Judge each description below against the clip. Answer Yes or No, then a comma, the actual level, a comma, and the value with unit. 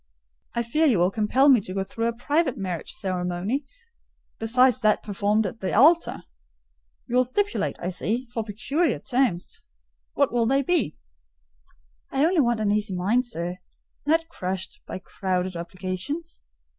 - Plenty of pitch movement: Yes, wide, 6.1 semitones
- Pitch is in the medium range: No, high, 220 Hz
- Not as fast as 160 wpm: Yes, average, 150 wpm